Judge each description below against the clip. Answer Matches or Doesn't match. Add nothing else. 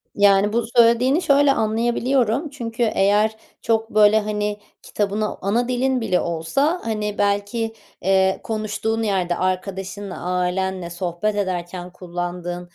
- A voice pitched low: Doesn't match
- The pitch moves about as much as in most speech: Matches